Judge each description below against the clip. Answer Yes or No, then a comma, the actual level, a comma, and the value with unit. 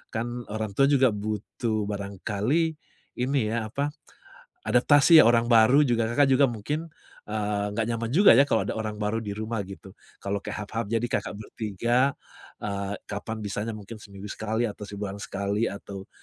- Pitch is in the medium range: No, low, 110 Hz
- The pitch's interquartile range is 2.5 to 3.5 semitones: Yes, average, 2.8 semitones